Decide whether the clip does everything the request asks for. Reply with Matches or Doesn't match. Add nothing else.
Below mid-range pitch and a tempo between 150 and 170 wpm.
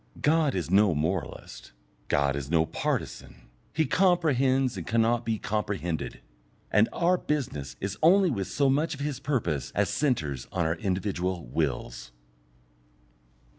Doesn't match